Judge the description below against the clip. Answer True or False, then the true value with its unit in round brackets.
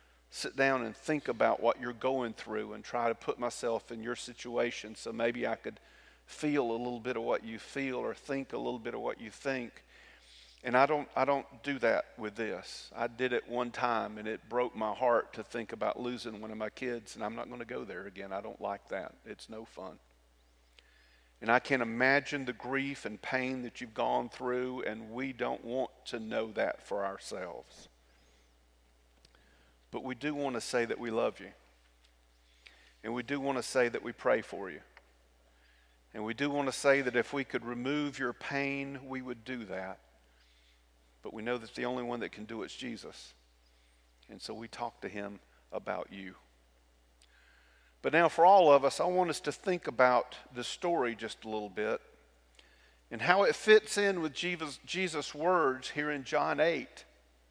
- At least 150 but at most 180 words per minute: False (200 wpm)